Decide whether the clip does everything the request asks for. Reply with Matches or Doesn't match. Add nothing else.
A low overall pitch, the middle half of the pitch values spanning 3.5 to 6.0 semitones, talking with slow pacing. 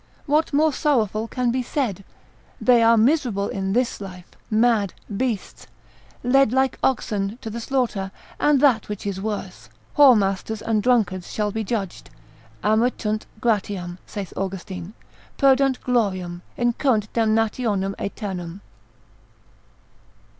Doesn't match